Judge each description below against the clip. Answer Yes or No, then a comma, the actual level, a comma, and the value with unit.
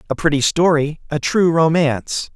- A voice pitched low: No, medium, 155 Hz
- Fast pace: No, average, 155 wpm